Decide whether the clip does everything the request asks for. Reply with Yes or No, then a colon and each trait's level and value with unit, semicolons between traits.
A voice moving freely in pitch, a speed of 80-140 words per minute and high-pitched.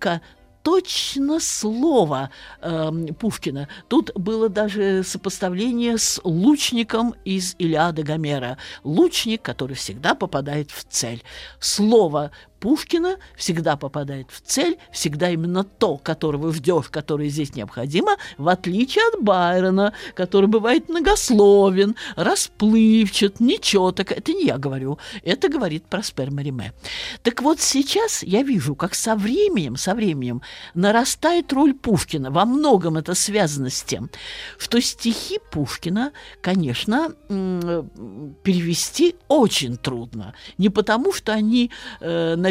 Yes: wide, 7.0 semitones; average, 115 wpm; high, 195 Hz